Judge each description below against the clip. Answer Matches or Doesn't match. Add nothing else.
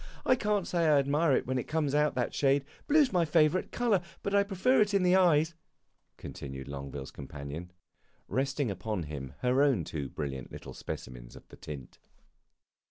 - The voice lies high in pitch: Doesn't match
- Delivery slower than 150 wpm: Doesn't match